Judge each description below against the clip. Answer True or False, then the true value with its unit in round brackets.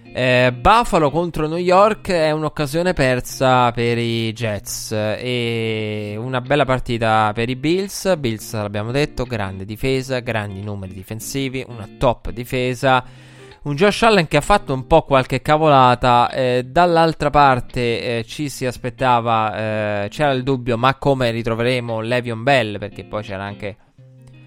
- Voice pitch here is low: True (125 Hz)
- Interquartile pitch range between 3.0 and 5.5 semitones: True (3.7 semitones)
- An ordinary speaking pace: True (145 wpm)